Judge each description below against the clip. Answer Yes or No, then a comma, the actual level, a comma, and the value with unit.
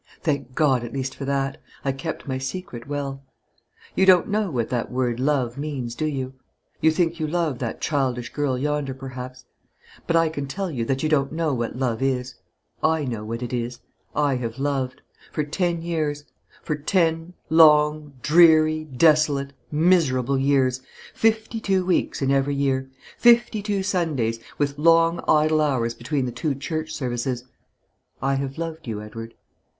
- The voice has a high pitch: No, medium, 140 Hz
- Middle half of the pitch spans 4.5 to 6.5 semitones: No, average, 3.7 semitones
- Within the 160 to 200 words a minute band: Yes, average, 165 wpm